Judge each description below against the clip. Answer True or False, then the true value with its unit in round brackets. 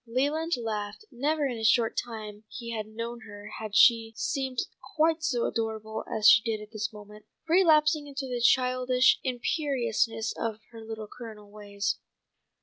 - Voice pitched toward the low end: False (230 Hz)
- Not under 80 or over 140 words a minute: False (155 wpm)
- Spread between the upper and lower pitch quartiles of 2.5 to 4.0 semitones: True (3.3 semitones)